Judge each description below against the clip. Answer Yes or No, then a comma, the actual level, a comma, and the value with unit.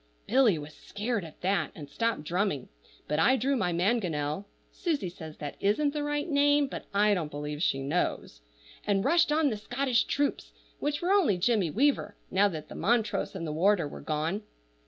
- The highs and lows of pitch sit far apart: Yes, wide, 8.8 semitones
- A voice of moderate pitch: No, high, 205 Hz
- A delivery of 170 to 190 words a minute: Yes, average, 180 wpm